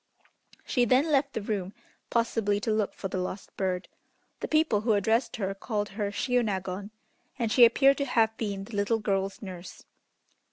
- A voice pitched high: Yes, high, 215 Hz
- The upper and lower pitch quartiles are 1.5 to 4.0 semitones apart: Yes, average, 3.3 semitones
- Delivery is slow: No, average, 170 wpm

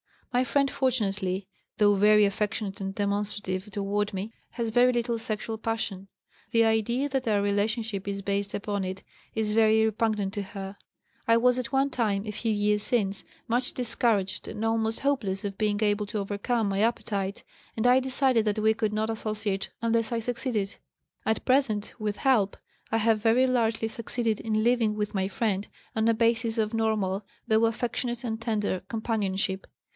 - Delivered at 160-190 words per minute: Yes, average, 170 wpm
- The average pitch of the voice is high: Yes, high, 220 Hz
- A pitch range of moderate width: No, narrow, 2.2 semitones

